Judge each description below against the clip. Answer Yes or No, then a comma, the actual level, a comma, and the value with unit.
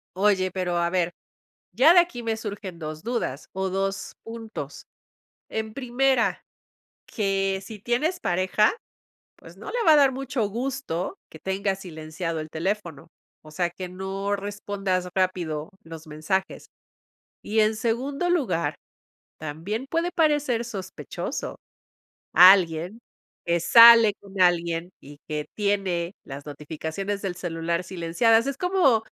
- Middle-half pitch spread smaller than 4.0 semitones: No, average, 5.1 semitones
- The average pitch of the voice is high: Yes, high, 195 Hz